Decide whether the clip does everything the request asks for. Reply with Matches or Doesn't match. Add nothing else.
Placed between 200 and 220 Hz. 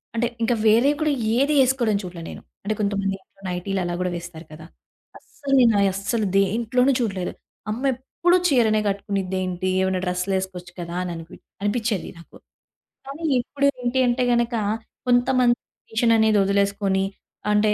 Matches